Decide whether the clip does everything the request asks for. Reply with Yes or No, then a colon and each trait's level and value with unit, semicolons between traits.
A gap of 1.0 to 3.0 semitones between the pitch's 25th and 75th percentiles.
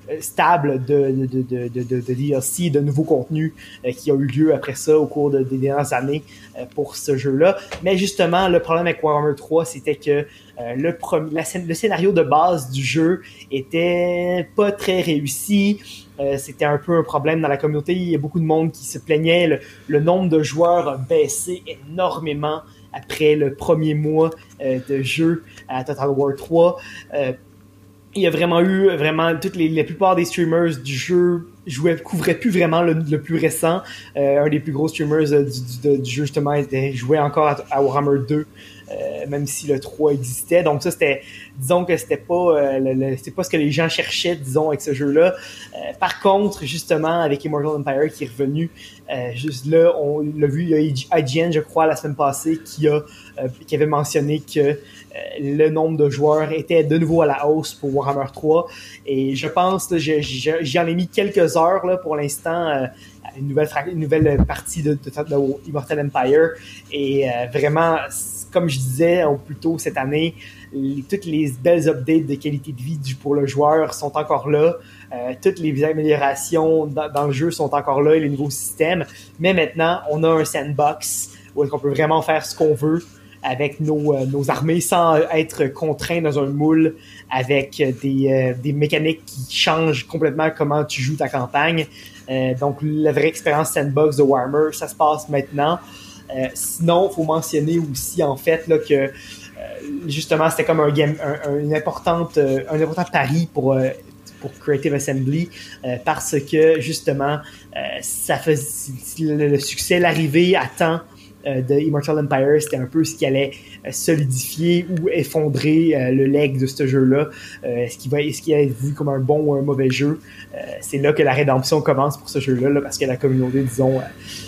Yes: average, 2.7 semitones